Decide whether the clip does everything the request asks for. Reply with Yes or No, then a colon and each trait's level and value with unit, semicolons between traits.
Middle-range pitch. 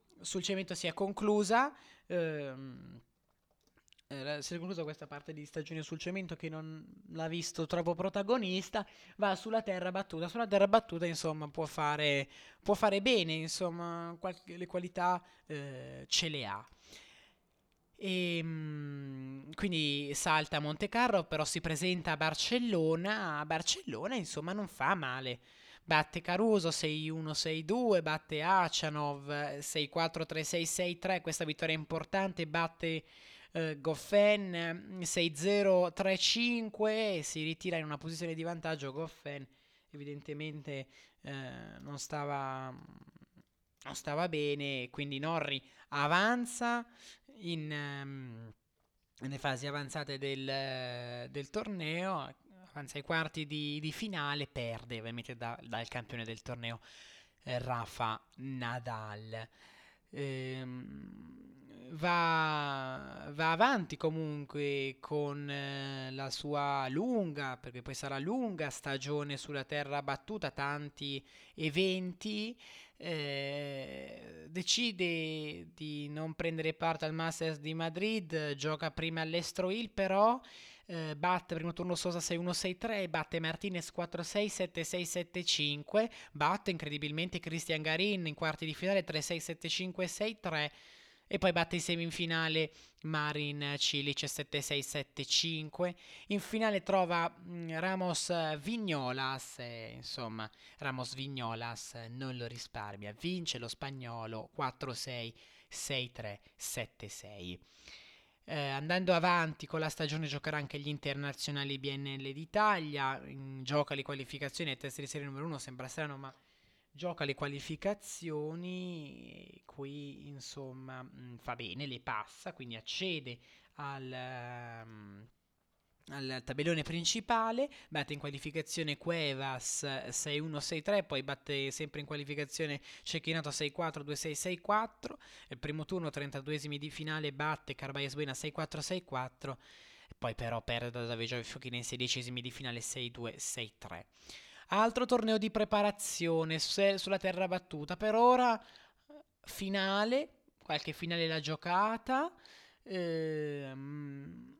Yes: medium, 155 Hz